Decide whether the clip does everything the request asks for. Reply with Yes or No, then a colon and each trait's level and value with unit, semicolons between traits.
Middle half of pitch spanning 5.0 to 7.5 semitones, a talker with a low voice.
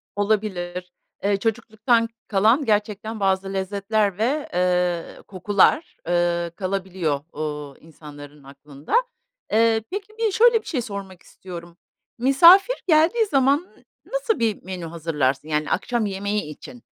No: average, 5.3 semitones; high, 200 Hz